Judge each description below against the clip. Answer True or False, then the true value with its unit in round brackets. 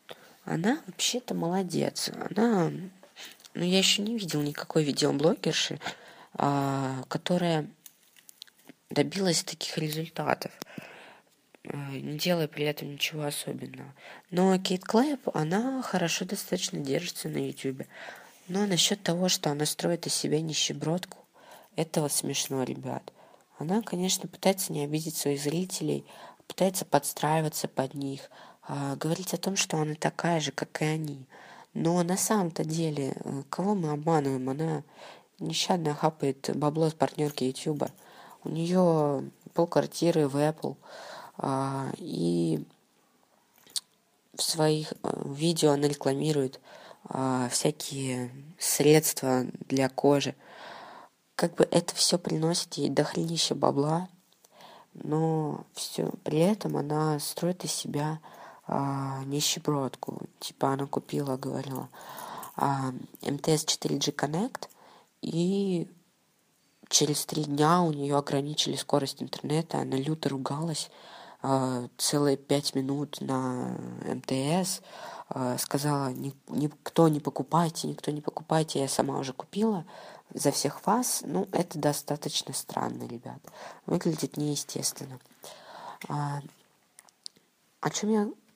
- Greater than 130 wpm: False (110 wpm)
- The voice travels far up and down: False (3.7 semitones)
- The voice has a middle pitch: True (150 Hz)